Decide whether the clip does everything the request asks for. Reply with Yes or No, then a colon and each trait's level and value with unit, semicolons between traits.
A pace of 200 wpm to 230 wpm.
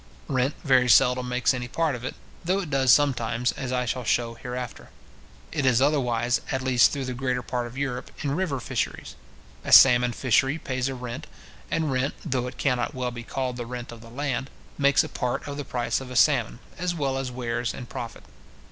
Yes: fast, 205 wpm